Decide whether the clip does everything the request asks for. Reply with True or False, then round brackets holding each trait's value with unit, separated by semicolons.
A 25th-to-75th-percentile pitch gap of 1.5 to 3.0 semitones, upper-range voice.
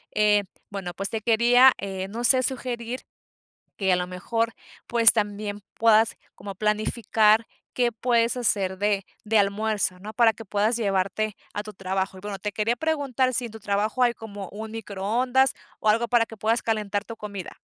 True (2.7 semitones; 215 Hz)